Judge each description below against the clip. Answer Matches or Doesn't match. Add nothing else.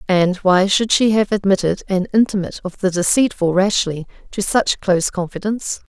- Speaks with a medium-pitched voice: Doesn't match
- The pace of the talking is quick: Doesn't match